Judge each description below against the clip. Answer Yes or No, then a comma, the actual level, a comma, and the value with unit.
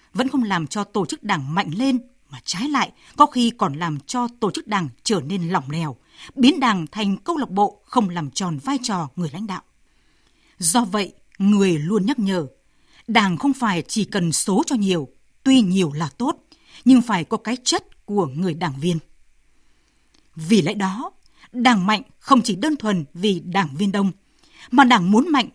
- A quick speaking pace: No, average, 195 wpm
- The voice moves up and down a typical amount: No, wide, 5.7 semitones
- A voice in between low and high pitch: No, high, 205 Hz